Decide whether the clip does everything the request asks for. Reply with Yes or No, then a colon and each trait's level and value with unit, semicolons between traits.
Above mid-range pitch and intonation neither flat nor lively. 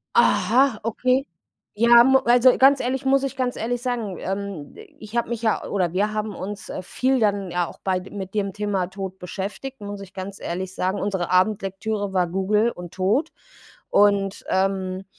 Yes: high, 205 Hz; average, 3.9 semitones